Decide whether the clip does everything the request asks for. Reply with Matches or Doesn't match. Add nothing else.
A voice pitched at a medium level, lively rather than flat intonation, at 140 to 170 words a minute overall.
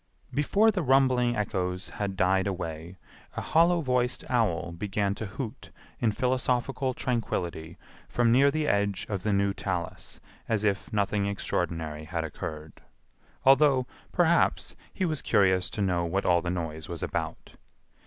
Doesn't match